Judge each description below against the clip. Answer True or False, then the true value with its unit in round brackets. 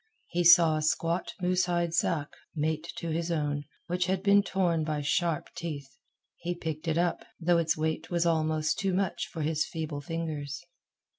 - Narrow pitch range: True (2.1 semitones)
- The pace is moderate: True (175 wpm)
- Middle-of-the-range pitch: True (165 Hz)